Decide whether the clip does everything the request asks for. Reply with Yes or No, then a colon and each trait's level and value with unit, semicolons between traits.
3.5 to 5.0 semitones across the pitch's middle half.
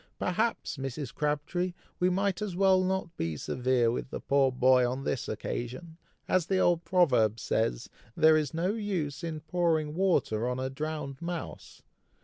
No: wide, 5.5 semitones